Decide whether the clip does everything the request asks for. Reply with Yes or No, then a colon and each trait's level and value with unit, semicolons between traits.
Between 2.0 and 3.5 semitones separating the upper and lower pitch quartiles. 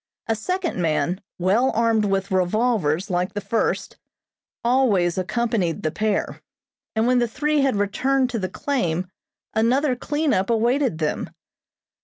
No: average, 5.3 semitones